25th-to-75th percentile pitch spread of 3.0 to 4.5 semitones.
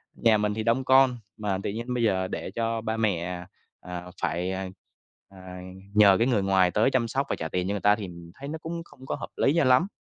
No: average, 4.9 semitones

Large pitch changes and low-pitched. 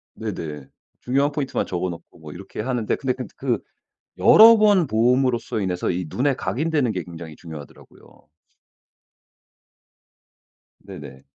Yes: wide, 7.7 semitones; low, 110 Hz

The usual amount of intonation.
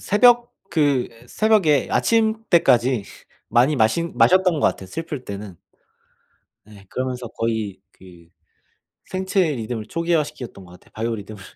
No: wide, 7.7 semitones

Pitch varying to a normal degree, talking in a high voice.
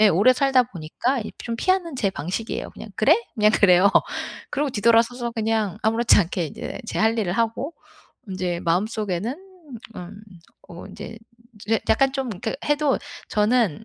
Yes: average, 4.0 semitones; high, 225 Hz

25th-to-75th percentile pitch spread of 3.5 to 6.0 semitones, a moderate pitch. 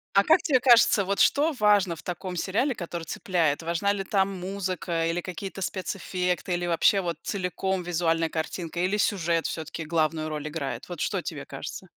No: average, 3.1 semitones; medium, 180 Hz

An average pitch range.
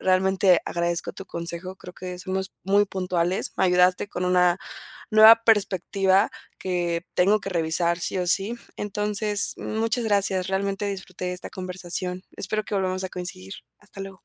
No: narrow, 1.7 semitones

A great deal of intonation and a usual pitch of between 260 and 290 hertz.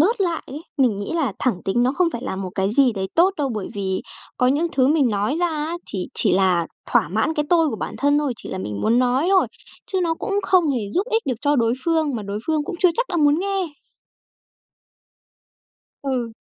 Yes: wide, 7.4 semitones; very high, 280 Hz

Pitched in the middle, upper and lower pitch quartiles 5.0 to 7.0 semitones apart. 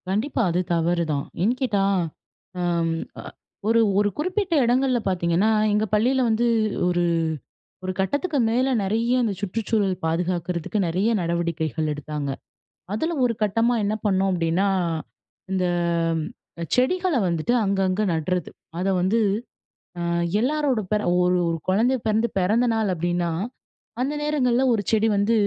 No: high, 205 Hz; wide, 5.4 semitones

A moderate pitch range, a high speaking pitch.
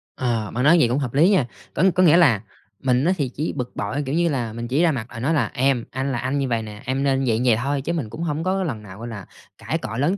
No: average, 4.3 semitones; low, 130 Hz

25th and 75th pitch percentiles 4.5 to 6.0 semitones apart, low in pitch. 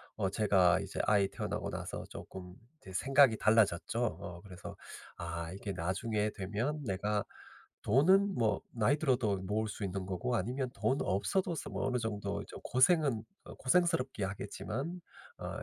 Yes: wide, 5.4 semitones; low, 110 Hz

